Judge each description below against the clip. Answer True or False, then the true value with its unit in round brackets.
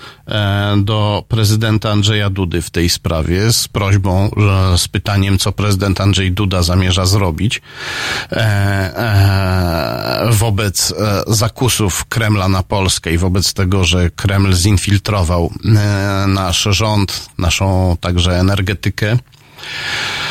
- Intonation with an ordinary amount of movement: False (2.2 semitones)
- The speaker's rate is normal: False (100 wpm)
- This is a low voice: True (100 Hz)